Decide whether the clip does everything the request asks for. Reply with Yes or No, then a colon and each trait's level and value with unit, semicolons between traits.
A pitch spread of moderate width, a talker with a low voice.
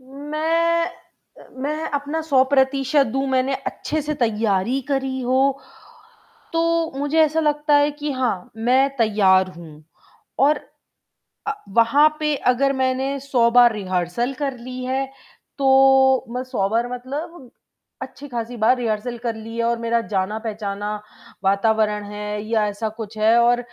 No: average, 4.0 semitones; very high, 255 Hz